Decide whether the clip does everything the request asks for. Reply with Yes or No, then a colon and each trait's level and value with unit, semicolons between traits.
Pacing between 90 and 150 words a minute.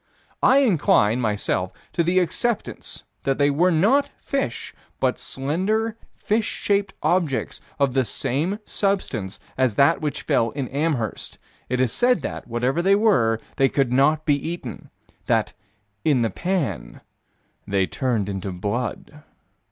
Yes: average, 140 wpm